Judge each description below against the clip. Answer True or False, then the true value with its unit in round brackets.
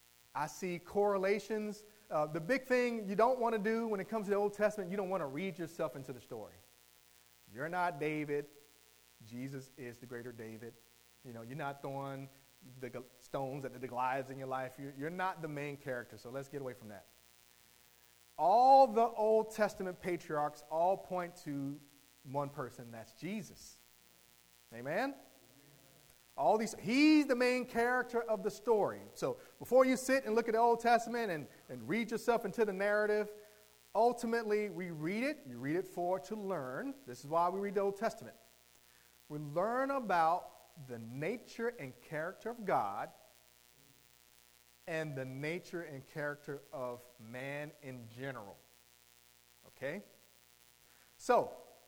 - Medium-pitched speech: True (150 Hz)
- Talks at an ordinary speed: True (160 wpm)